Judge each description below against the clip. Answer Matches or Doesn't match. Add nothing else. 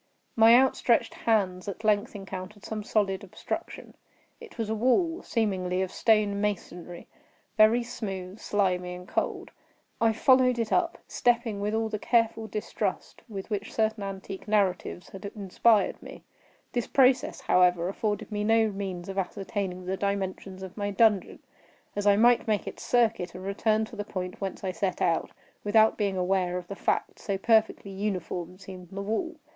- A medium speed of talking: Matches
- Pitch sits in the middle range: Doesn't match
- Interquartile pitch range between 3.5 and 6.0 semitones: Doesn't match